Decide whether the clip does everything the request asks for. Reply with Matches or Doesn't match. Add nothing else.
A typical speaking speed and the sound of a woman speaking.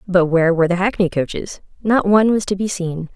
Doesn't match